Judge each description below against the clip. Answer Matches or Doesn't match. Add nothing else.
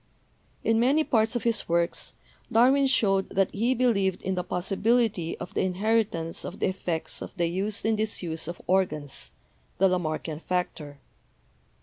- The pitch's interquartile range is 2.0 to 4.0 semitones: Doesn't match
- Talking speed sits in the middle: Matches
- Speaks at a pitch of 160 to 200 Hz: Matches